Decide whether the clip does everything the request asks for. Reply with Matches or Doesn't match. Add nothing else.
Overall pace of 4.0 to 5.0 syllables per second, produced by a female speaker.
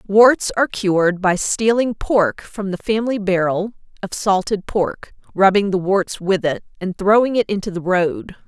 Matches